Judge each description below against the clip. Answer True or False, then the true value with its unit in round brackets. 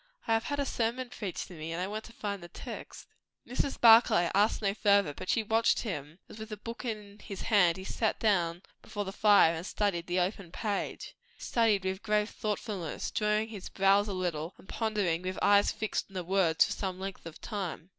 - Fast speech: True (215 wpm)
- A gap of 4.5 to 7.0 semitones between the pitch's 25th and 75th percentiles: False (3.2 semitones)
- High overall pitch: True (200 Hz)